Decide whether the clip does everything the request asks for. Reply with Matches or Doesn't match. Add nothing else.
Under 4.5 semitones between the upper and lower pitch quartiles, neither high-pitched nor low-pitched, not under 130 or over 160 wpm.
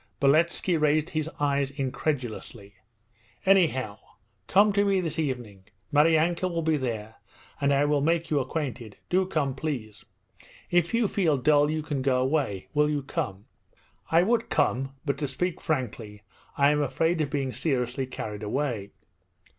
Matches